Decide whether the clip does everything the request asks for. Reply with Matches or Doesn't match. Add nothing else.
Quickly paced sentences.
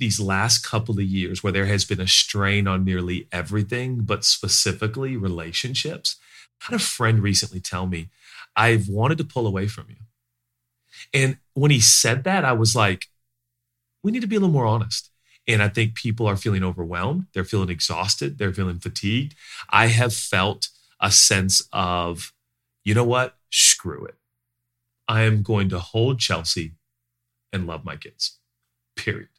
Doesn't match